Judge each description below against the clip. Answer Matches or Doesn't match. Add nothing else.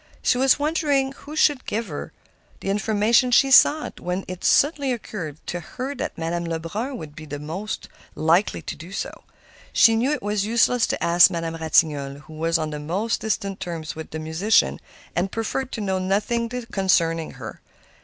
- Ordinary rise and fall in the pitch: Doesn't match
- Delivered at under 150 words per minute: Doesn't match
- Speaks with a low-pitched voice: Doesn't match